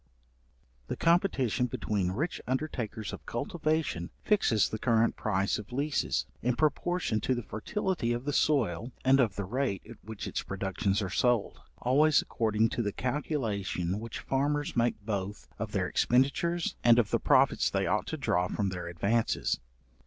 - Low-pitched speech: Yes, low, 120 Hz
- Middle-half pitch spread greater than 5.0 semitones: Yes, wide, 5.5 semitones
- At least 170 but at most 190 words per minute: No, average, 160 wpm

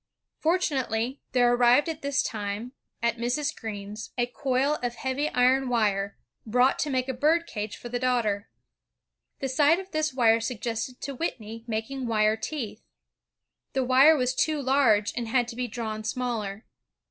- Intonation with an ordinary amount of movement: Yes, average, 3.3 semitones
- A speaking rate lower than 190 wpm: Yes, average, 165 wpm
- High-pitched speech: Yes, high, 245 Hz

